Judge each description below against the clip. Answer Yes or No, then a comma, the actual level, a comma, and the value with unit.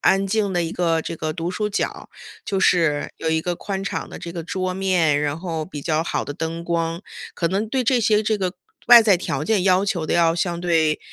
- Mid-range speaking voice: Yes, medium, 175 Hz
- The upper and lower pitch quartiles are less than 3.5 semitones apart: Yes, average, 3.1 semitones